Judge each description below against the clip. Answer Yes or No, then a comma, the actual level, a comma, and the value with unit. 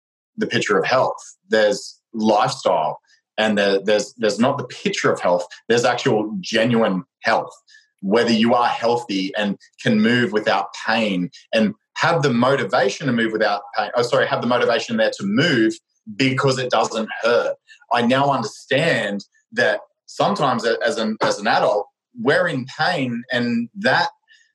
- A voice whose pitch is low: Yes, low, 120 Hz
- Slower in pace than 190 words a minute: Yes, average, 155 wpm